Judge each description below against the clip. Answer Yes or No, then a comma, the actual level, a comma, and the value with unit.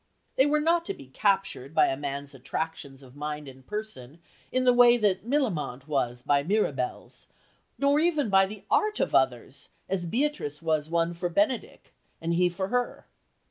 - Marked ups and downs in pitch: Yes, wide, 9.0 semitones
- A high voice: No, medium, 175 Hz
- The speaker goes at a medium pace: Yes, average, 175 wpm